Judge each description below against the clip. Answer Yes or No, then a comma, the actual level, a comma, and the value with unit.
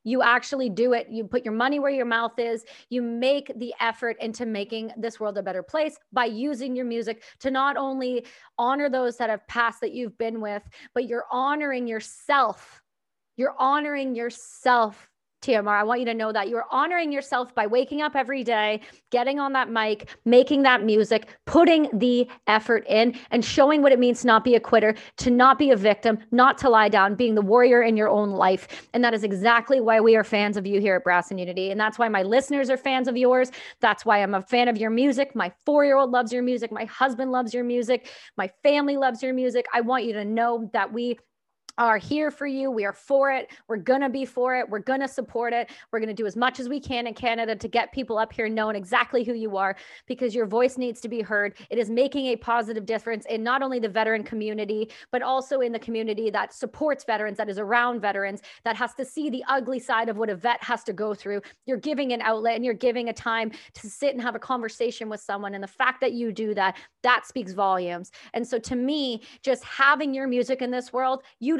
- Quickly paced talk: Yes, fast, 235 wpm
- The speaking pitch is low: No, high, 240 Hz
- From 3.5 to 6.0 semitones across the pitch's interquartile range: No, average, 2.7 semitones